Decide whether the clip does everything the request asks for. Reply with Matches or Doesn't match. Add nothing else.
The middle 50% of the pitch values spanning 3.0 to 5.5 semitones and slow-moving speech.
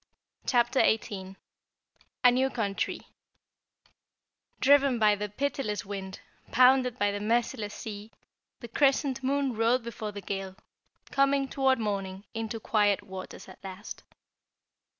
Matches